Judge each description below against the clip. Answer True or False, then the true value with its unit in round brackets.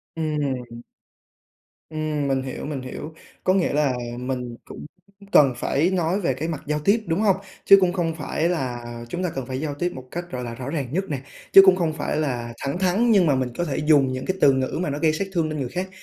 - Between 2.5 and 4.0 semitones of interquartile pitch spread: False (4.8 semitones)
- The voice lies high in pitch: False (150 Hz)